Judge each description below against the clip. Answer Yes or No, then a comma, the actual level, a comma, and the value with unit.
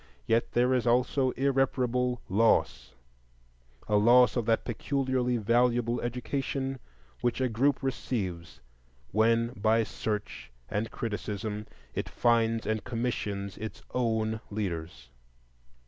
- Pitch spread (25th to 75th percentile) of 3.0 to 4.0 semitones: Yes, average, 3.3 semitones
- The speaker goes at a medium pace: No, slow, 105 wpm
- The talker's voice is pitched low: Yes, low, 115 Hz